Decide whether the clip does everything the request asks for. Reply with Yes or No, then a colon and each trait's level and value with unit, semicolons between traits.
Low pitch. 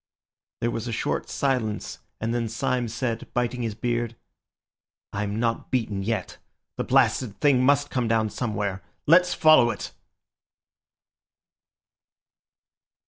Yes: low, 120 Hz